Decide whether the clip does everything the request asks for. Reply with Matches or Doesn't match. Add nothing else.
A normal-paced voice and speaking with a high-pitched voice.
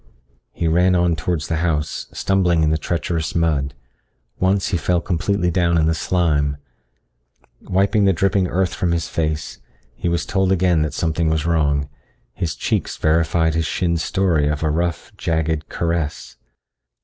Doesn't match